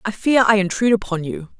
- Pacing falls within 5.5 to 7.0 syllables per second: Yes, 6.4 syllables/s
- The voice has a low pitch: No, high, 205 Hz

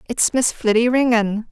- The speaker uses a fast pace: No, average, 160 wpm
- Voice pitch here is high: Yes, high, 230 Hz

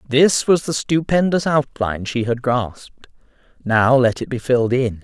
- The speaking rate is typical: Yes, average, 165 wpm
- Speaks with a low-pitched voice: Yes, low, 130 Hz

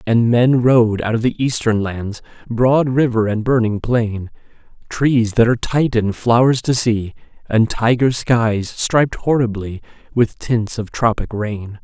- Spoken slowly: No, average, 150 wpm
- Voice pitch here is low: Yes, low, 115 Hz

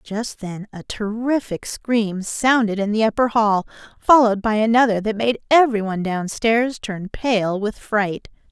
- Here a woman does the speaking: Yes, female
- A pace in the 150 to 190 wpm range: Yes, average, 160 wpm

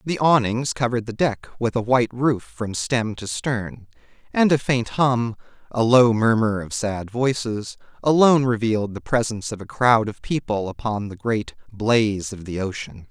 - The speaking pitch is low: Yes, low, 115 Hz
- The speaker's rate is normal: Yes, average, 180 wpm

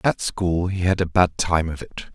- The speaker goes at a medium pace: No, fast, 250 wpm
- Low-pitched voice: Yes, very low, 90 Hz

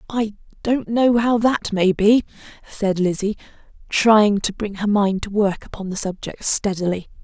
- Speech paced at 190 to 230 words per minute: No, average, 165 wpm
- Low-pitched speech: No, high, 205 Hz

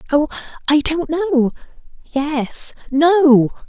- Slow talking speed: Yes, slow, 50 wpm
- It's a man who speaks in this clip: No, female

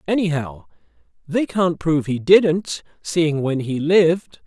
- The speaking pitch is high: No, medium, 160 Hz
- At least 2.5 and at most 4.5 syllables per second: Yes, 4.0 syllables/s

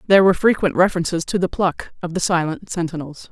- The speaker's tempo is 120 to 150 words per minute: No, average, 200 wpm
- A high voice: No, medium, 175 Hz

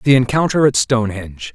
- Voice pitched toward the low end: Yes, low, 120 Hz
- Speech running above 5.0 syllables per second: Yes, 6.0 syllables/s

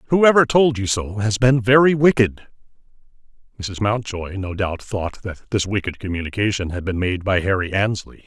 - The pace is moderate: Yes, average, 165 wpm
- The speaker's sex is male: Yes, male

